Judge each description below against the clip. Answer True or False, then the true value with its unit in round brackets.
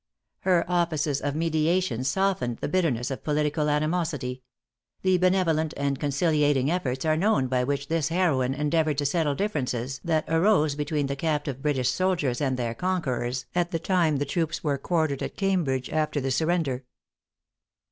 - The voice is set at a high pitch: False (150 Hz)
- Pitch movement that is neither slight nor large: True (3.8 semitones)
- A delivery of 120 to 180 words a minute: True (155 wpm)